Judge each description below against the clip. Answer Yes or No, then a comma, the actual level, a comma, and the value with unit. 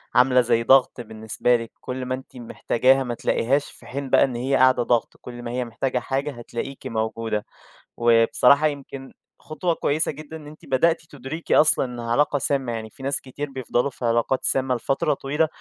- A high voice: No, low, 130 Hz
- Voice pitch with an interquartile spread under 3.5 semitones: Yes, average, 2.8 semitones